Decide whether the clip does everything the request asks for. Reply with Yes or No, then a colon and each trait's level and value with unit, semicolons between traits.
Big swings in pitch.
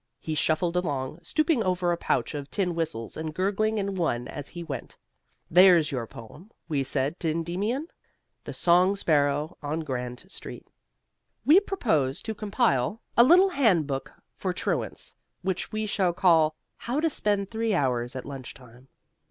Yes: wide, 6.2 semitones